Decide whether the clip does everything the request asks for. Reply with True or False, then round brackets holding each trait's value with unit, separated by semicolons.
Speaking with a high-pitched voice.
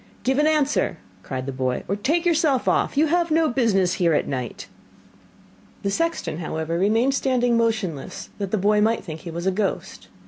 True (210 Hz)